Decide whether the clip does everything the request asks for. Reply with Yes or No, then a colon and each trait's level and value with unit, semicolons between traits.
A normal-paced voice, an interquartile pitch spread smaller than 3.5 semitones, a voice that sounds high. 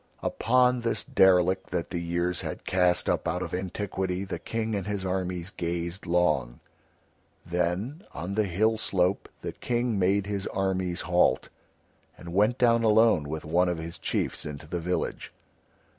No: average, 160 wpm; average, 3.0 semitones; very low, 90 Hz